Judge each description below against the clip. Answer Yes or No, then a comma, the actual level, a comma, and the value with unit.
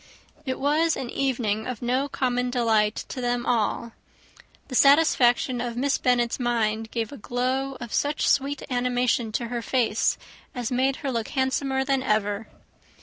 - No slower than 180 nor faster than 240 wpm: No, average, 155 wpm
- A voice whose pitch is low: No, high, 245 Hz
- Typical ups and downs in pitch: No, narrow, 2.2 semitones